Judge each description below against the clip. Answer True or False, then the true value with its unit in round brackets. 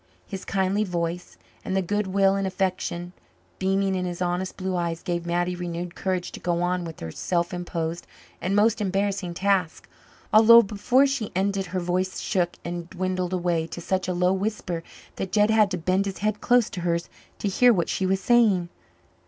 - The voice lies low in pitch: False (185 Hz)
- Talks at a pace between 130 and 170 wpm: False (190 wpm)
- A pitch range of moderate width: False (2.1 semitones)